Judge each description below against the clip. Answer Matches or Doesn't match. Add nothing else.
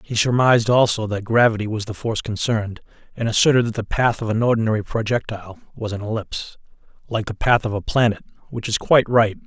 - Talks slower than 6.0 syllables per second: Doesn't match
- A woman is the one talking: Doesn't match